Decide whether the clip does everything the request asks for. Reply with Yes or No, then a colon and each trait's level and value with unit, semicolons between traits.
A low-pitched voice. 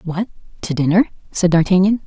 No: medium, 185 Hz